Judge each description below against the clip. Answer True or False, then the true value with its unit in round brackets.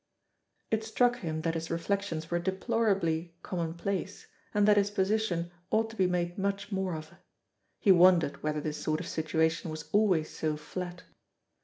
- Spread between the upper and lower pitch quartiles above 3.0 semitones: True (3.8 semitones)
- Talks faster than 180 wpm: False (160 wpm)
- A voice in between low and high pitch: True (175 Hz)